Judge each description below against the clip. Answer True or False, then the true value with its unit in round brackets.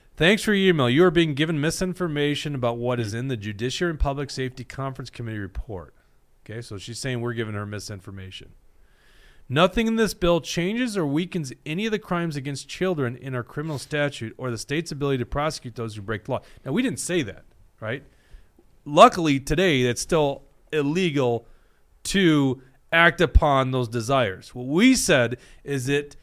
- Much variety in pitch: True (5.7 semitones)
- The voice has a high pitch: False (140 Hz)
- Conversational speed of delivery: True (180 wpm)